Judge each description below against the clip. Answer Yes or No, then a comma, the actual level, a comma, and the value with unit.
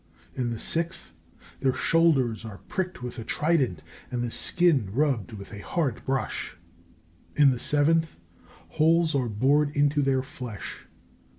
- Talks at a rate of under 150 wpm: Yes, average, 140 wpm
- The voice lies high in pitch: No, low, 135 Hz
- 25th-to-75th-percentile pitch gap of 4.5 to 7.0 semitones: Yes, average, 5.1 semitones